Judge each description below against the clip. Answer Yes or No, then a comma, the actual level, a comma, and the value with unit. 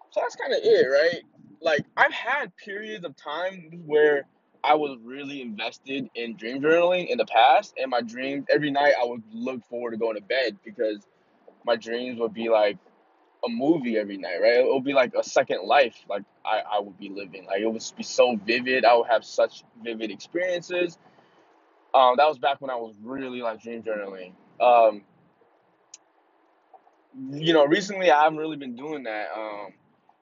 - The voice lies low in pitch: Yes, low, 125 Hz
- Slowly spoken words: No, average, 185 wpm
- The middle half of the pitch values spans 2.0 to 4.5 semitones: No, average, 5.0 semitones